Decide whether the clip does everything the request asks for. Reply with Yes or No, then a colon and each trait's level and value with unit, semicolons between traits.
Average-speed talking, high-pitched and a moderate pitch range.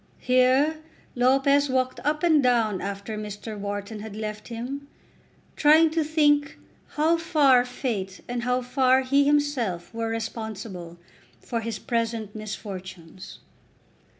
No: slow, 125 wpm; high, 245 Hz; average, 4.9 semitones